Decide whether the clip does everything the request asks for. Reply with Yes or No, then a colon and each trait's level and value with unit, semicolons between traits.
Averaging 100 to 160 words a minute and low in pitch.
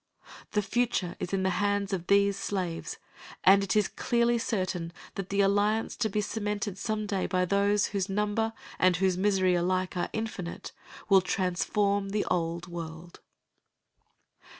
No: average, 150 wpm; high, 195 Hz